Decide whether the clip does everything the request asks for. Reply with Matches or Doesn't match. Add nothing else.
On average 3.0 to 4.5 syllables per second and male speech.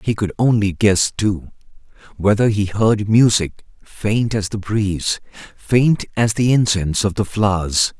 Matches